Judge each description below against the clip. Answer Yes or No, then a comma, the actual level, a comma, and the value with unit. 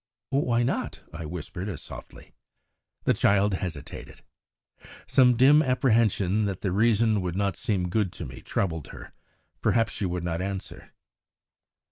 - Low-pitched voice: Yes, low, 100 Hz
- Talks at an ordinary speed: Yes, average, 145 wpm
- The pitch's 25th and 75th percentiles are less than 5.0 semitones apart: Yes, average, 4.4 semitones